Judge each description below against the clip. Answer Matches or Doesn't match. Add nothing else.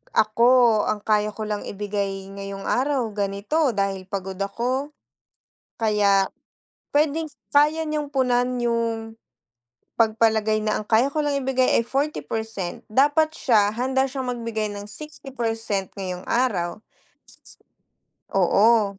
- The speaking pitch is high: Matches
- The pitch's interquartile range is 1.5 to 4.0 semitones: Doesn't match